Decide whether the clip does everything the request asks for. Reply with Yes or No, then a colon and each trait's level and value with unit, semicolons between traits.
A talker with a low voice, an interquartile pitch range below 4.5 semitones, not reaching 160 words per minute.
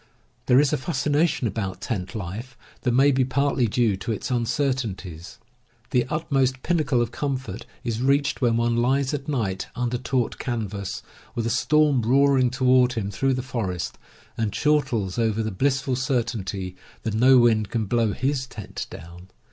No: low, 120 Hz; average, 3.4 semitones; average, 165 wpm